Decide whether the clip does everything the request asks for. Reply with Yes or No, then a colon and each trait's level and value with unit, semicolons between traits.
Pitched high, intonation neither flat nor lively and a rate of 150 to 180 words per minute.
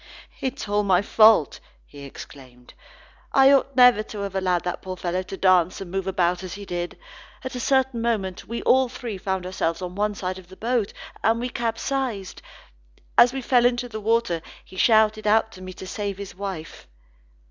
No: high, 200 Hz; average, 4.2 semitones; average, 195 wpm